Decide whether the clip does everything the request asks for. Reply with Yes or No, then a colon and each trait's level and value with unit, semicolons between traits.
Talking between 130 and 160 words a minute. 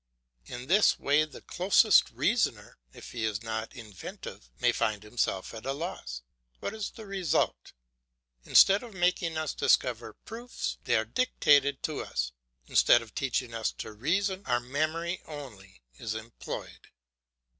Yes: average, 145 wpm